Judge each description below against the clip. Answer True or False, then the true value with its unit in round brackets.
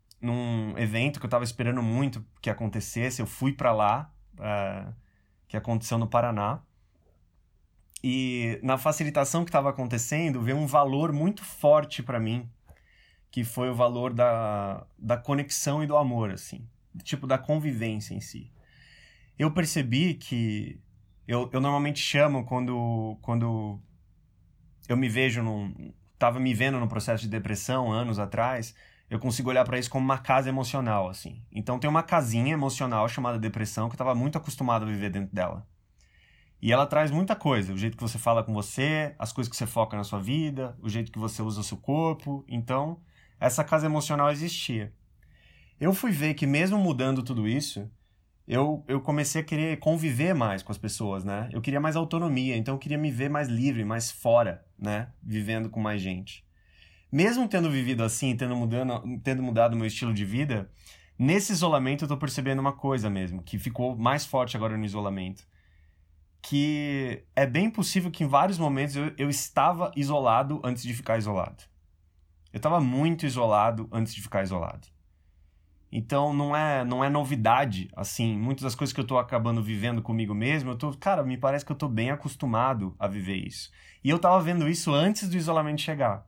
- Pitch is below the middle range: True (120 Hz)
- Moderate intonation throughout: True (5.0 semitones)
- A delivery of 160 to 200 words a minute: True (175 wpm)